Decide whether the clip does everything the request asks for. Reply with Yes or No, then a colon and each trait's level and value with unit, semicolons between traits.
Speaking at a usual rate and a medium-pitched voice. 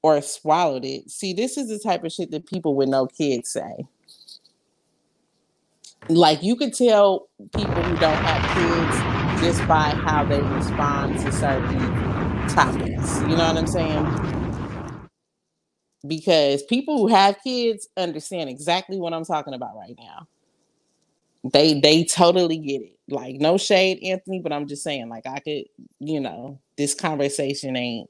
Yes: average, 155 wpm; medium, 160 Hz